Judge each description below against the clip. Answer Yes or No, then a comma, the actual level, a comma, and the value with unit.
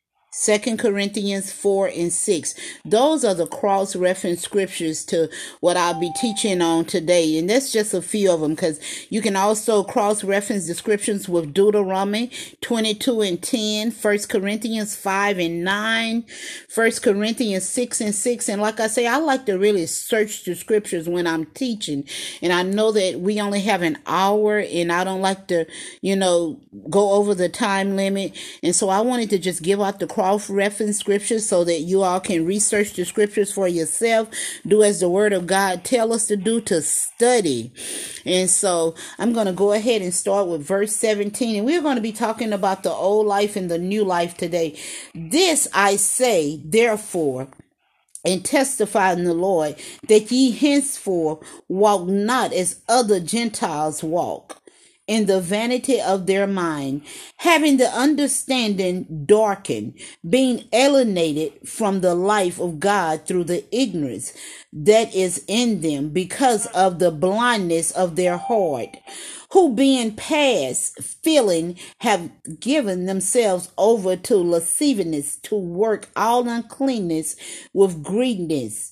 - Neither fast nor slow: Yes, average, 155 wpm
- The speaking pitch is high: Yes, high, 200 Hz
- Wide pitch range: No, average, 4.1 semitones